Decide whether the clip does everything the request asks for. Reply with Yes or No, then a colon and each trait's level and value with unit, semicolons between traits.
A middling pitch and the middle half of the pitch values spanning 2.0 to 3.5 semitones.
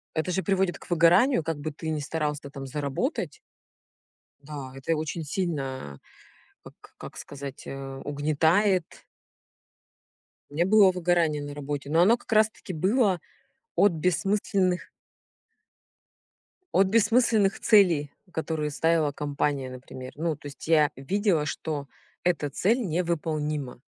No: medium, 160 Hz; average, 4.2 semitones